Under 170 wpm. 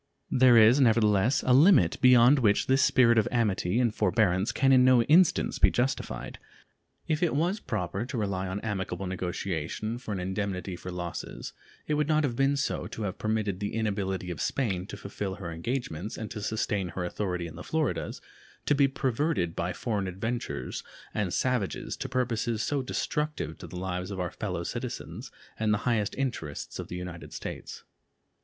No: average, 180 wpm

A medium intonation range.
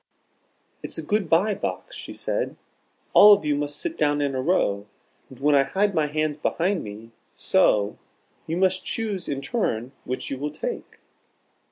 No: wide, 6.1 semitones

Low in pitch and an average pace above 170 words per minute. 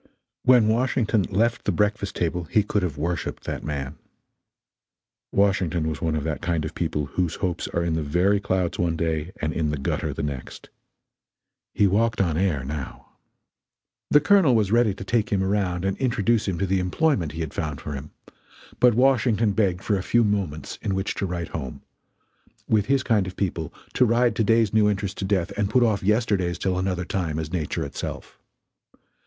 Yes: very low, 95 Hz; average, 195 wpm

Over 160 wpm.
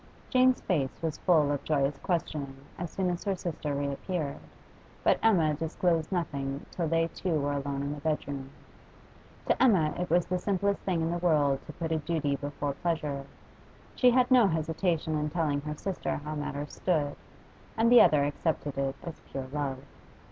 Yes: average, 180 wpm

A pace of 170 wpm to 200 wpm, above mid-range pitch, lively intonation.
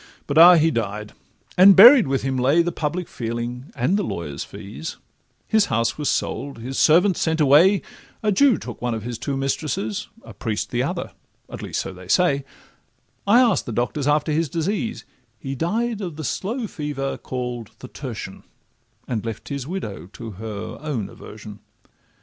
No: average, 175 wpm; medium, 140 Hz; wide, 7.3 semitones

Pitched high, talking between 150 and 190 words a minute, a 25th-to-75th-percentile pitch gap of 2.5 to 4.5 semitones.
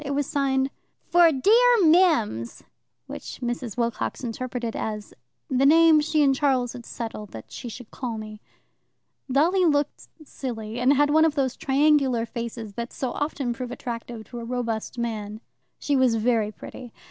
Yes: very high, 255 Hz; average, 160 wpm; average, 3.9 semitones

